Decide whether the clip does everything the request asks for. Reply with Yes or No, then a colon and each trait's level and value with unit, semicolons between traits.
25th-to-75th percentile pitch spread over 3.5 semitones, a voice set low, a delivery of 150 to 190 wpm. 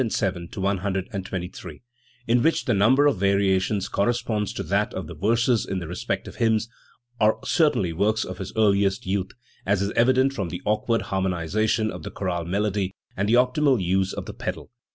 No: average, 3.1 semitones; low, 100 Hz; average, 175 wpm